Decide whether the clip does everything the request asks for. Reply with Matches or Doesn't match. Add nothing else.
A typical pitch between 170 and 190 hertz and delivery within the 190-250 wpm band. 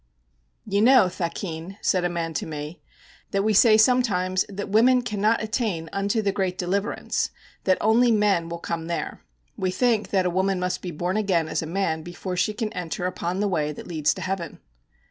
Matches